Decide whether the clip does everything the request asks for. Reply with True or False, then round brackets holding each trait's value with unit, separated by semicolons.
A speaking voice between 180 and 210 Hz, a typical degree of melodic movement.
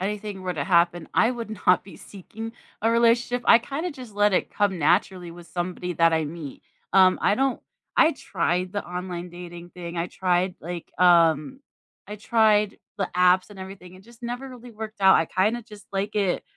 True (190 Hz; 3.8 semitones)